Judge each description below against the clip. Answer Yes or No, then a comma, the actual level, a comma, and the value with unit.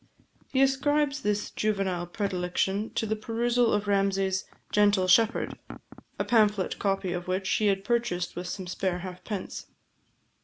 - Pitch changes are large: No, average, 3.3 semitones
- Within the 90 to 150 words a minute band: Yes, average, 140 wpm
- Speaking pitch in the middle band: No, high, 200 Hz